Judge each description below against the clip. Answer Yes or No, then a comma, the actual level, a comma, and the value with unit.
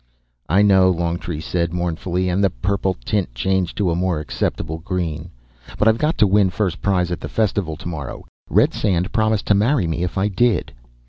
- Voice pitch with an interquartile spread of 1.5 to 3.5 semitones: Yes, average, 3.0 semitones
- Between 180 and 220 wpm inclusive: Yes, average, 185 wpm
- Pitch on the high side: No, very low, 90 Hz